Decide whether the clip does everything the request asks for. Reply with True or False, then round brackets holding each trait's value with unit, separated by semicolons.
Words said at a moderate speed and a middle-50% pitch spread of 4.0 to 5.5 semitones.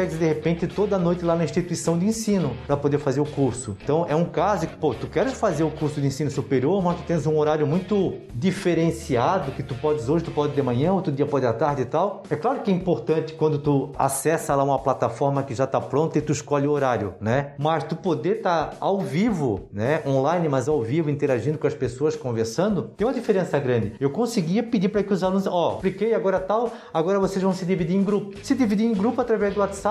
False (235 wpm; 5.1 semitones)